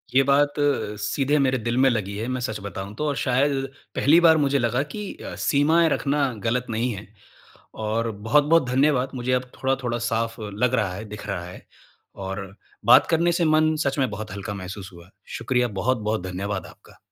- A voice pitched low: Yes, low, 125 Hz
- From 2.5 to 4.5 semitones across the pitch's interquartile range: No, average, 5.0 semitones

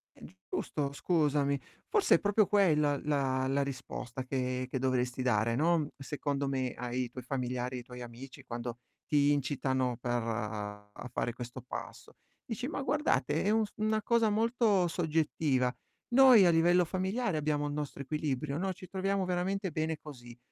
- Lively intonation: Yes, wide, 6.2 semitones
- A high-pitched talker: No, medium, 145 Hz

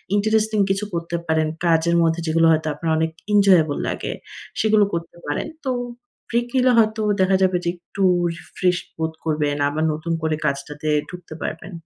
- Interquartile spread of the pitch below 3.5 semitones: No, average, 3.9 semitones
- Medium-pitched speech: Yes, medium, 170 Hz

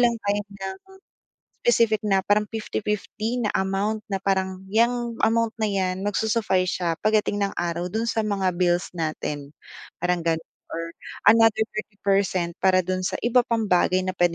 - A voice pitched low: No, high, 200 Hz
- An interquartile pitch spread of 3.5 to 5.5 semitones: No, average, 3.1 semitones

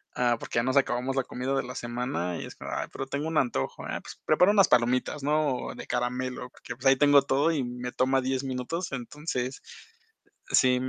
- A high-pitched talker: No, low, 130 Hz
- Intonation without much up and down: Yes, narrow, 2.3 semitones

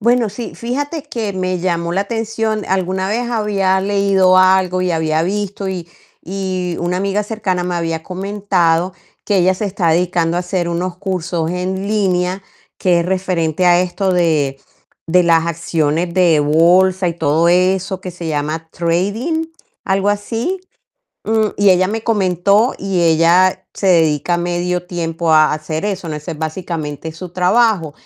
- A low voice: No, medium, 185 Hz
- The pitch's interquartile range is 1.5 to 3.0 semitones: Yes, average, 2.7 semitones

